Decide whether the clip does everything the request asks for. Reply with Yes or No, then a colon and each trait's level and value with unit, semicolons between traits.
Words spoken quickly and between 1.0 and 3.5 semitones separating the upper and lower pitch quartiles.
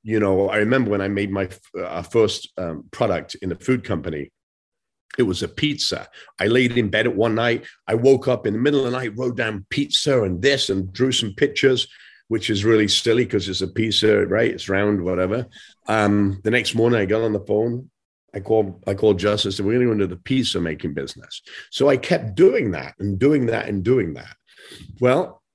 No: fast, 215 wpm; average, 3.9 semitones